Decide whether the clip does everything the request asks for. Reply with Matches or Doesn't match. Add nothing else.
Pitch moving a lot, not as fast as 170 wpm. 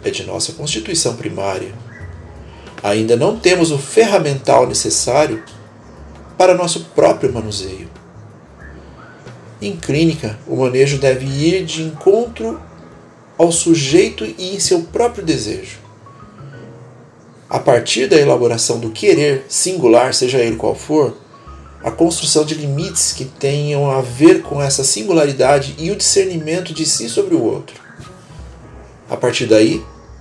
Matches